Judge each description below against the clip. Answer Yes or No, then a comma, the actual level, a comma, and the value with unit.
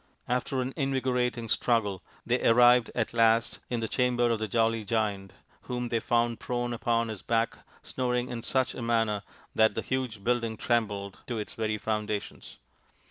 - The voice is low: Yes, low, 115 Hz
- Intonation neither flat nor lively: No, narrow, 1.9 semitones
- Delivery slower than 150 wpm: No, average, 165 wpm